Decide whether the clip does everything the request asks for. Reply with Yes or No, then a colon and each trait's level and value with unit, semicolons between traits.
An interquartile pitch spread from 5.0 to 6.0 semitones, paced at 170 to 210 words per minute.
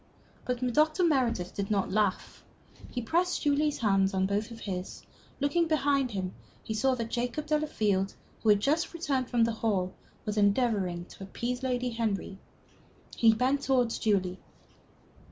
No: average, 5.3 semitones; average, 155 wpm